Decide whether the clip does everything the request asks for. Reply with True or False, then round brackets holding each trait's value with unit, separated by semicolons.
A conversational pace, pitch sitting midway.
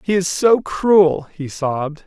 True (175 wpm; 170 Hz)